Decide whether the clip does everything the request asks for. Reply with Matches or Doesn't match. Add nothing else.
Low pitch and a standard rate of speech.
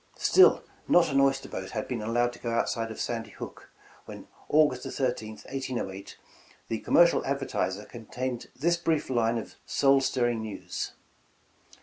Matches